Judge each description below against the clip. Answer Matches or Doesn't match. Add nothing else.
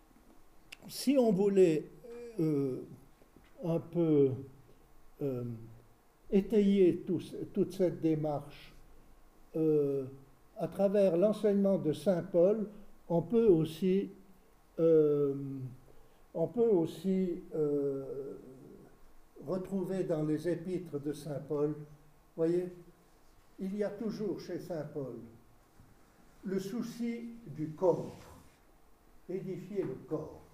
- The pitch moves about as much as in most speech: Matches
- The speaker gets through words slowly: Matches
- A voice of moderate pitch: Matches